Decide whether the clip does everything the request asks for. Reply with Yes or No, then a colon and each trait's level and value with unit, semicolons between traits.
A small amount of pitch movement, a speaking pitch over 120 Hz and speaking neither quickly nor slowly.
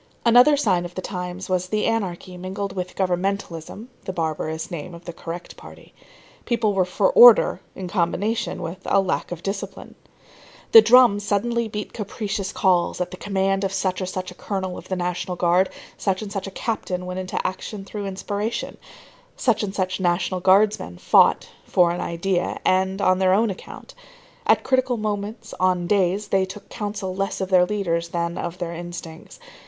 Yes: narrow, 2.3 semitones; high, 190 Hz; average, 175 wpm